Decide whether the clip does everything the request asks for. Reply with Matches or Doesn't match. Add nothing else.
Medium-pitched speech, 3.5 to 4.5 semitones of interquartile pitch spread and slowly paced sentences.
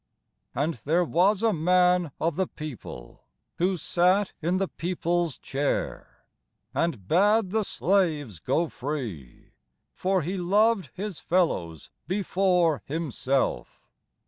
Matches